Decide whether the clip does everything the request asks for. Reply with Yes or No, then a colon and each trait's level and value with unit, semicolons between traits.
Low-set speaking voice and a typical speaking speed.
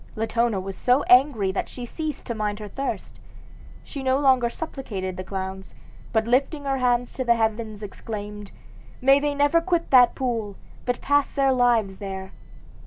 No: high, 240 Hz; average, 165 wpm